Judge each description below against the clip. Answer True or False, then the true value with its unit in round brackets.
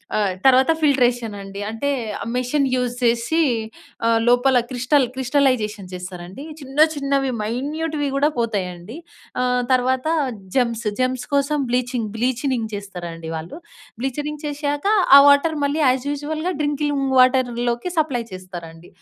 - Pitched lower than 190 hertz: False (255 Hz)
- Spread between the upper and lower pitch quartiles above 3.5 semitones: True (4.0 semitones)